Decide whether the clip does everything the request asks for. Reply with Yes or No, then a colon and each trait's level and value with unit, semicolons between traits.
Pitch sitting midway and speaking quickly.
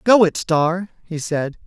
No: medium, 170 Hz; average, 180 wpm